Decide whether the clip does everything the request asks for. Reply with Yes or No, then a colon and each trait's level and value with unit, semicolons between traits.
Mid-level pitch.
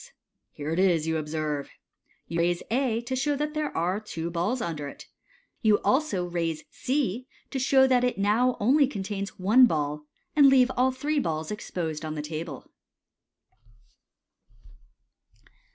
No: high, 200 Hz